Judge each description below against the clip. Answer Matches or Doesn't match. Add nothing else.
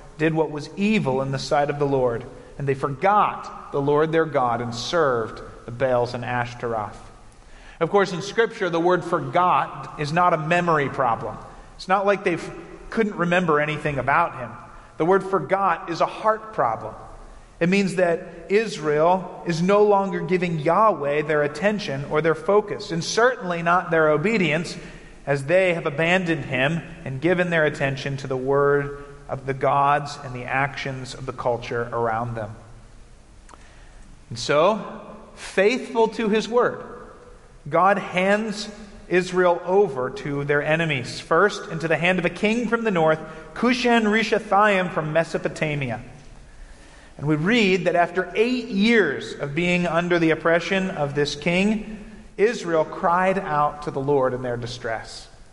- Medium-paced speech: Matches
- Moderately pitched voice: Matches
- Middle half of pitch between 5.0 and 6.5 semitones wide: Matches